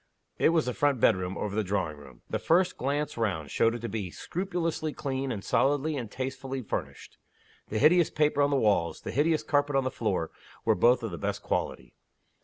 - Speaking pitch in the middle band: No, low, 130 Hz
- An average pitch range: No, wide, 6.1 semitones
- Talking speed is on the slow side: No, fast, 205 wpm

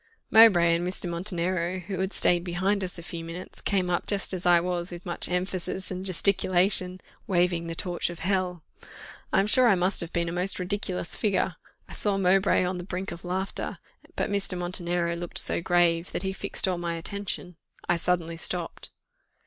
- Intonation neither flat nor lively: No, narrow, 1.7 semitones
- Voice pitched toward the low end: No, medium, 180 Hz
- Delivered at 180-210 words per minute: Yes, average, 190 wpm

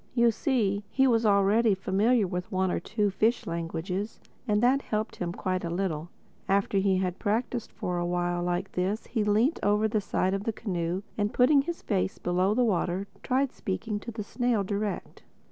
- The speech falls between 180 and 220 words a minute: Yes, average, 190 wpm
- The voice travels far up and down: No, average, 3.5 semitones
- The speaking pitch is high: Yes, high, 200 Hz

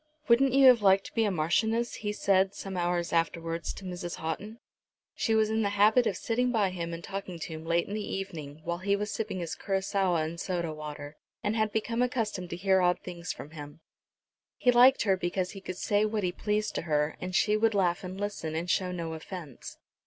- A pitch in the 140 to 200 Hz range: Yes, high, 190 Hz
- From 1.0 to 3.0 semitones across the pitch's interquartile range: No, average, 3.8 semitones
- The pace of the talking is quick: Yes, fast, 220 wpm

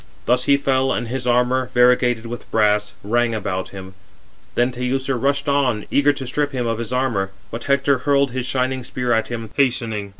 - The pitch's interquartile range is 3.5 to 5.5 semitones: No, narrow, 2.5 semitones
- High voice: No, low, 125 Hz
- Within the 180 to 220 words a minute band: Yes, average, 190 wpm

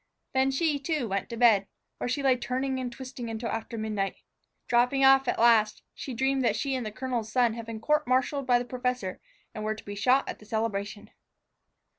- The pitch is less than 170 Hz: No, high, 245 Hz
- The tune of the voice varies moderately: Yes, average, 3.2 semitones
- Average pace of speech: No, fast, 210 wpm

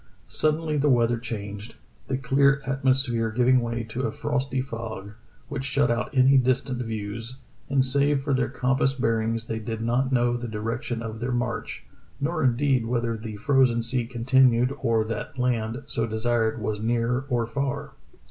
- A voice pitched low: Yes, low, 120 Hz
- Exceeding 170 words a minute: No, average, 165 wpm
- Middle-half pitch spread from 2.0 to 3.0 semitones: Yes, average, 2.7 semitones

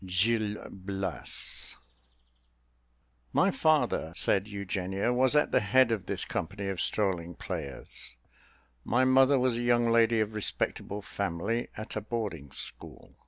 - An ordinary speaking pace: No, slow, 130 wpm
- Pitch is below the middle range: Yes, low, 105 Hz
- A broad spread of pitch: No, average, 3.7 semitones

